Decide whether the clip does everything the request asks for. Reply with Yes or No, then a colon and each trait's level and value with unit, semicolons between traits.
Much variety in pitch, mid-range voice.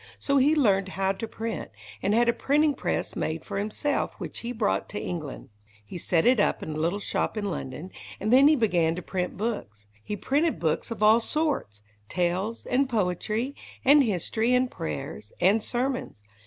No: wide, 5.9 semitones; high, 210 Hz